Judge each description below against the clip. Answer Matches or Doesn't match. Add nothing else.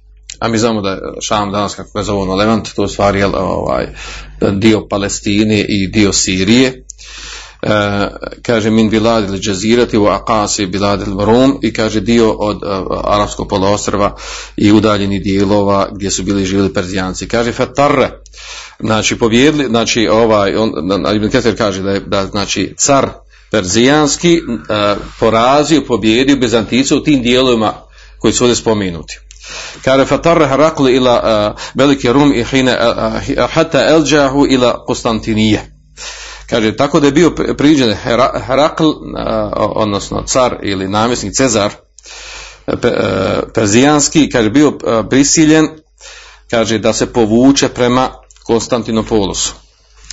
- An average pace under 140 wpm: Matches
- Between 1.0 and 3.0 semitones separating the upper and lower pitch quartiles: Doesn't match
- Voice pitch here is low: Matches